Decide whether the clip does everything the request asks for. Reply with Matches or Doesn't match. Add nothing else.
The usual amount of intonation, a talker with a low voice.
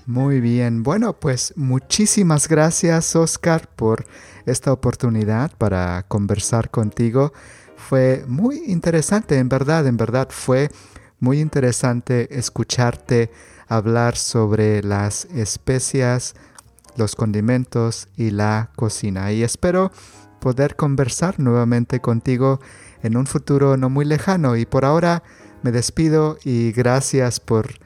Matches